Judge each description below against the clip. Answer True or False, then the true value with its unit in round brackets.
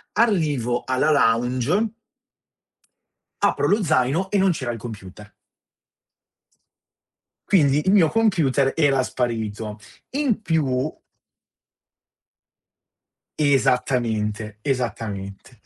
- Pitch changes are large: True (5.9 semitones)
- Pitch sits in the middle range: False (130 Hz)